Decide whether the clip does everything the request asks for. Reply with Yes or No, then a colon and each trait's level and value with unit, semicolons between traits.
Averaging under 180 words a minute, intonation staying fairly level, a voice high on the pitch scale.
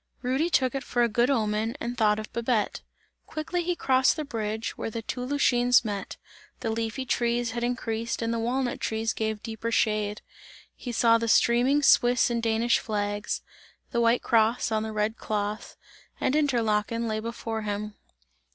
Yes: average, 170 wpm; narrow, 2.2 semitones; high, 230 Hz